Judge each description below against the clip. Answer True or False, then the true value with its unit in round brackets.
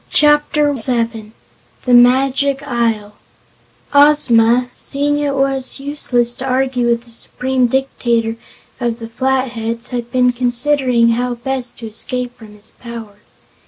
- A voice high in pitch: True (245 Hz)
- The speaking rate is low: True (125 wpm)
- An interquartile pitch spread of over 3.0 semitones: False (2.4 semitones)